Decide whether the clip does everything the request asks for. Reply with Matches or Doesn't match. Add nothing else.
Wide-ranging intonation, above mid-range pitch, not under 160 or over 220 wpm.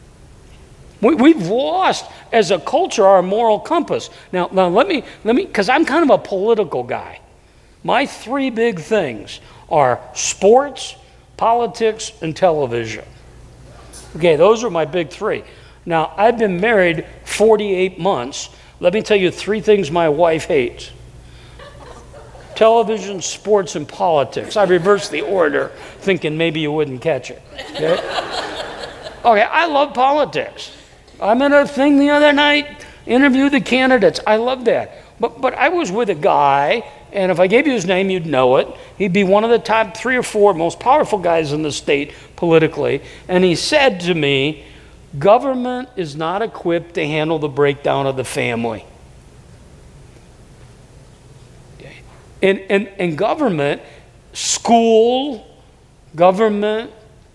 Doesn't match